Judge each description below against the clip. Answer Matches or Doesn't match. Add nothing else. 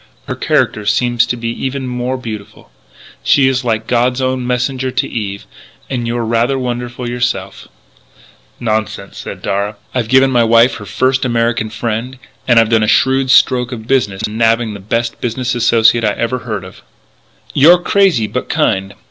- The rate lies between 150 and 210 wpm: Matches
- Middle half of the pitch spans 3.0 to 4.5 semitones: Doesn't match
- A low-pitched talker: Matches